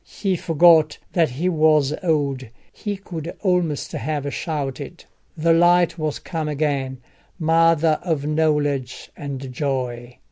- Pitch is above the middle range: No, medium, 155 Hz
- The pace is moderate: No, slow, 120 wpm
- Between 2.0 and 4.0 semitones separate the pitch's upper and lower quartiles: Yes, average, 3.0 semitones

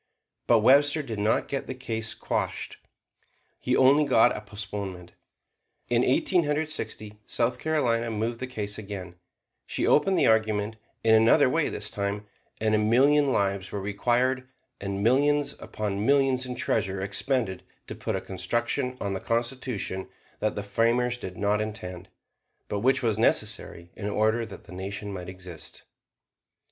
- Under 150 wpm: No, average, 155 wpm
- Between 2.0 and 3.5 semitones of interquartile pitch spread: No, average, 4.1 semitones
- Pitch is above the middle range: No, low, 110 Hz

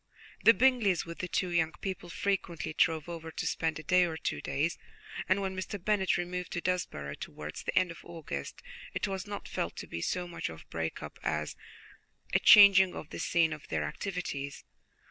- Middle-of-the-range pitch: Yes, medium, 175 Hz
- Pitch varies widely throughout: No, average, 3.0 semitones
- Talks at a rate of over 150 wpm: Yes, average, 200 wpm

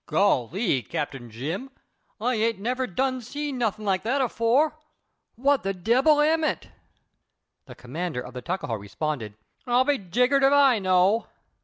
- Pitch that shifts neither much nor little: No, wide, 6.9 semitones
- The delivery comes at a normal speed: Yes, average, 150 wpm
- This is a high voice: Yes, high, 225 Hz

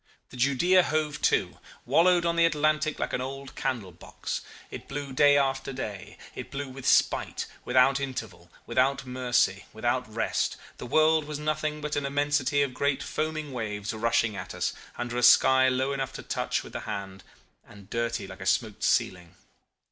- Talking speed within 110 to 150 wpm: No, average, 170 wpm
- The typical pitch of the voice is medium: No, low, 130 Hz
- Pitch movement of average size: Yes, average, 3.8 semitones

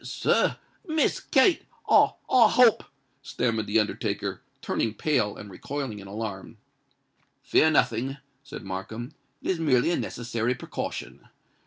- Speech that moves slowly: Yes, slow, 115 wpm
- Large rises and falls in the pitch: Yes, wide, 6.4 semitones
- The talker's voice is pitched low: Yes, low, 125 Hz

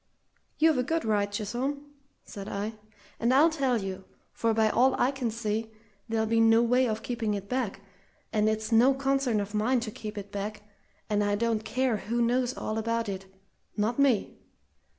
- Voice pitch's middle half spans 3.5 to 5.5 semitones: No, average, 3.1 semitones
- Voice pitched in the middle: No, high, 225 Hz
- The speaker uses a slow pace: No, average, 185 wpm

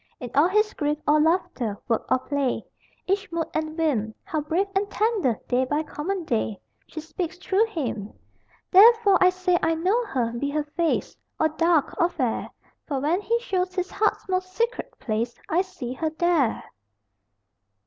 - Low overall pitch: No, very high, 325 Hz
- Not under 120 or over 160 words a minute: No, average, 170 wpm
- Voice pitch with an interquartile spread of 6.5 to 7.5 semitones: No, average, 5.1 semitones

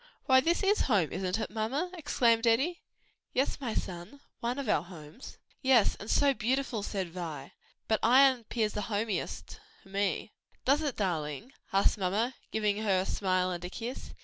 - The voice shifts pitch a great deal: Yes, wide, 5.9 semitones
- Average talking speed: Yes, average, 175 wpm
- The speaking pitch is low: No, high, 220 Hz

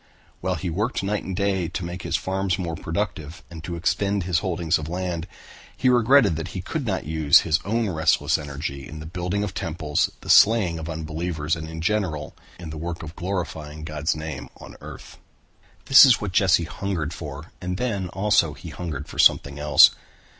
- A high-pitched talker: No, very low, 85 Hz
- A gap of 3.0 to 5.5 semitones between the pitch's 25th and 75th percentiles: Yes, average, 3.5 semitones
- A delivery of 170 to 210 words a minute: Yes, average, 190 wpm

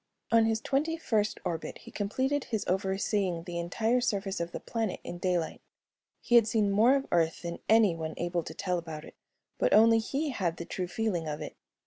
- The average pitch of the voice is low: No, high, 200 Hz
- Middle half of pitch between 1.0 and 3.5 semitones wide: No, average, 4.7 semitones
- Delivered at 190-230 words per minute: Yes, average, 195 wpm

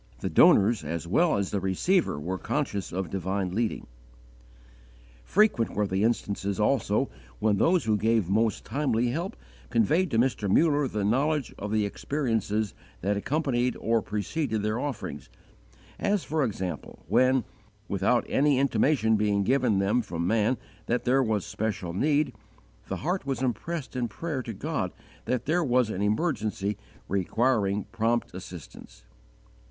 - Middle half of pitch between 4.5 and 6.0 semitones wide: Yes, average, 5.0 semitones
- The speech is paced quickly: No, average, 145 wpm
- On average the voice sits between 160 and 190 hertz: No, low, 115 Hz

